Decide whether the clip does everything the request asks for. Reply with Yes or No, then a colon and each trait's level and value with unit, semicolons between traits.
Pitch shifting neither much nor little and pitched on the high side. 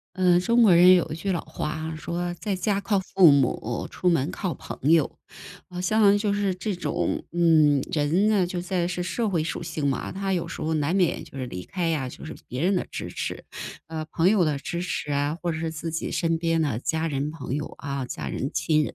No: average, 3.2 semitones; medium, 165 Hz